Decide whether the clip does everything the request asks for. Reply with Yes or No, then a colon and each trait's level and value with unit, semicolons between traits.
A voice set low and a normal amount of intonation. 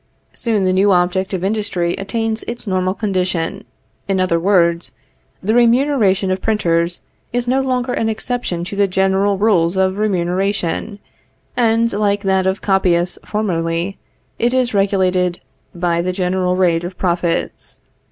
No: high, 190 Hz; average, 3.1 semitones